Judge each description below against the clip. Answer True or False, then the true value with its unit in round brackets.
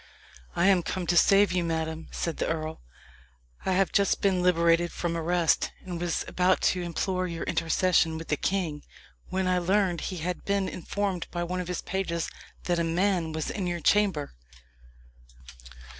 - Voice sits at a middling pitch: True (175 Hz)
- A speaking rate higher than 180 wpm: False (175 wpm)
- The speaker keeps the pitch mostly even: True (2.0 semitones)